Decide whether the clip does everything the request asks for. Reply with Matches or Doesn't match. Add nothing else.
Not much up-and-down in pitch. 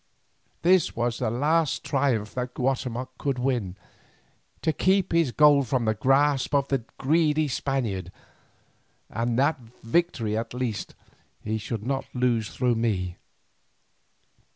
Doesn't match